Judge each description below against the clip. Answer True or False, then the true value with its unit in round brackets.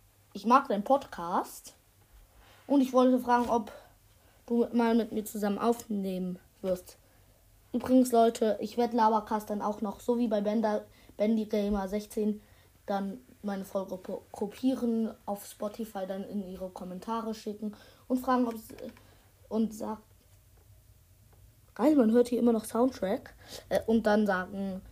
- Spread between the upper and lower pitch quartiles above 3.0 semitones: True (3.4 semitones)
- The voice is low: False (215 Hz)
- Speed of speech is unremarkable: True (140 wpm)